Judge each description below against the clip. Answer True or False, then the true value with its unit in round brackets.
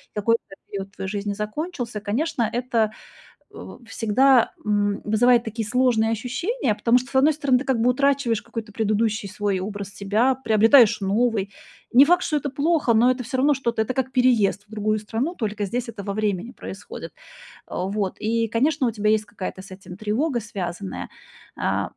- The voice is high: True (225 Hz)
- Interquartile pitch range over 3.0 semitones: True (3.6 semitones)